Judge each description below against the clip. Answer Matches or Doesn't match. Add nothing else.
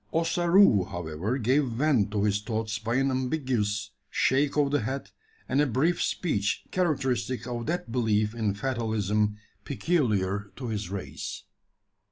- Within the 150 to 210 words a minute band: Doesn't match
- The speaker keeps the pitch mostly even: Doesn't match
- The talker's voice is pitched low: Matches